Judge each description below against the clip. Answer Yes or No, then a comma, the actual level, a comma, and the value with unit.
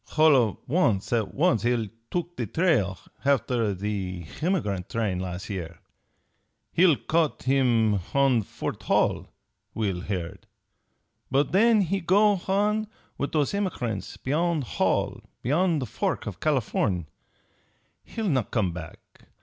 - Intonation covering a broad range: Yes, wide, 8.9 semitones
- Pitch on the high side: No, low, 130 Hz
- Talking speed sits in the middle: No, slow, 130 wpm